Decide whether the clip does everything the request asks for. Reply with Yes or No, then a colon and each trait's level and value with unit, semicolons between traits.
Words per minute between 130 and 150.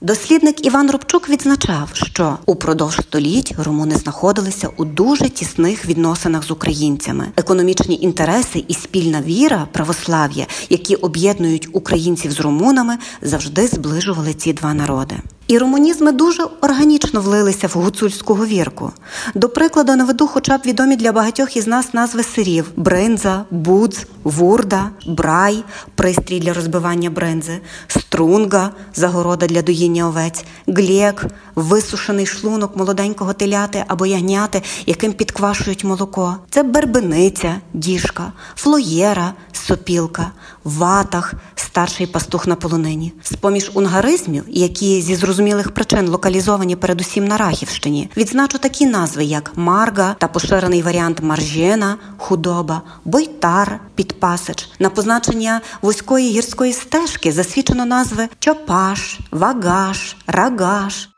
No: average, 115 wpm